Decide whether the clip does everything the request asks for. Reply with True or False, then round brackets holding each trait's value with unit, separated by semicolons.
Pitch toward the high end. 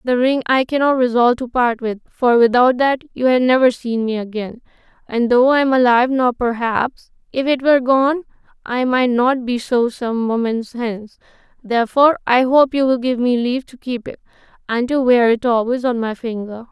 True (245 Hz)